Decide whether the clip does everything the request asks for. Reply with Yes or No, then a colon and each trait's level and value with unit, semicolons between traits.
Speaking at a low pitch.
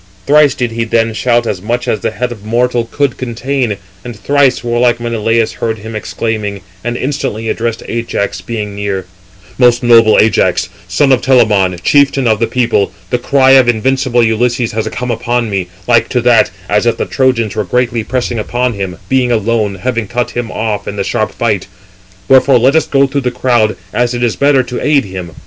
Yes: low, 120 Hz